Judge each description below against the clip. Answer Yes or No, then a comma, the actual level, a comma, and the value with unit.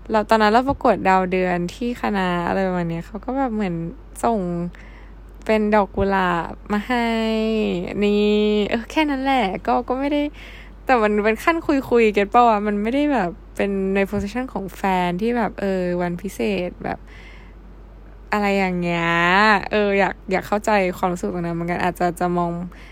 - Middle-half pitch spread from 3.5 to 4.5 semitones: Yes, average, 4.0 semitones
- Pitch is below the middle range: No, high, 205 Hz